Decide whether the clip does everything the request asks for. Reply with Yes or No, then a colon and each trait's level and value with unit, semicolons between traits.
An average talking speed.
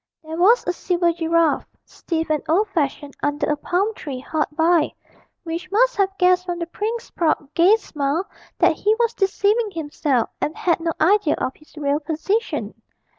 Yes: average, 175 wpm